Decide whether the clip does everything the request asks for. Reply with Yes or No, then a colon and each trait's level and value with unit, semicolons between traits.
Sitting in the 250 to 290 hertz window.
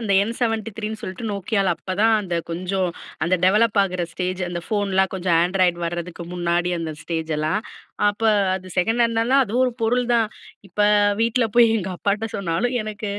No: high, 195 Hz